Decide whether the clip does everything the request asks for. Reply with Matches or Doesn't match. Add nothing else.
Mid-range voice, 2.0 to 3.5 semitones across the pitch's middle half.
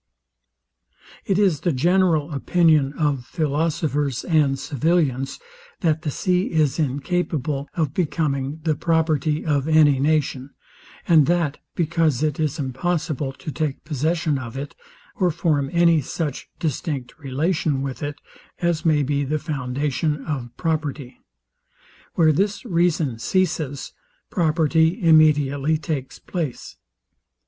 Matches